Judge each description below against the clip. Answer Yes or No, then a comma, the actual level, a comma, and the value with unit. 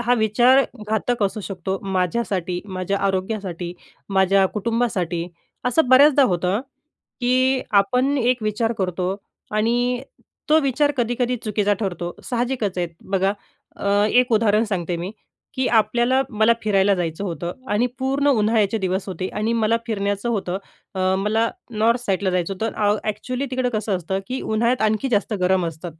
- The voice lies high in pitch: Yes, high, 210 Hz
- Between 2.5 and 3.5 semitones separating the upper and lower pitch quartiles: No, average, 4.2 semitones